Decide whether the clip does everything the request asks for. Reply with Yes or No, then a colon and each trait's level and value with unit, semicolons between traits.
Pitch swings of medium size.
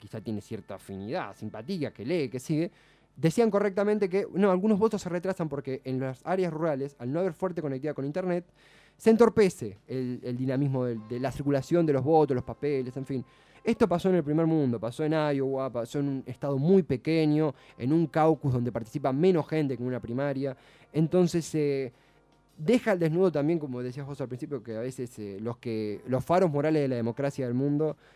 Yes: average, 4.6 semitones